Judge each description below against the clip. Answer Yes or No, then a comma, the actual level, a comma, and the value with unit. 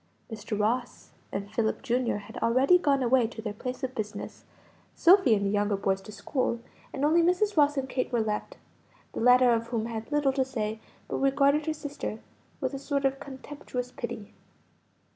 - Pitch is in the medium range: No, very high, 250 Hz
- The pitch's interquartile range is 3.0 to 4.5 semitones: Yes, average, 4.1 semitones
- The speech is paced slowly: No, average, 185 wpm